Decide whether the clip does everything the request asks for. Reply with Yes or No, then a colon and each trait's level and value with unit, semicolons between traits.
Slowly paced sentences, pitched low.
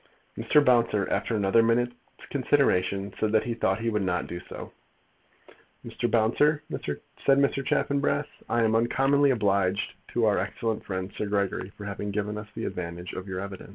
No: average, 170 wpm; low, 105 Hz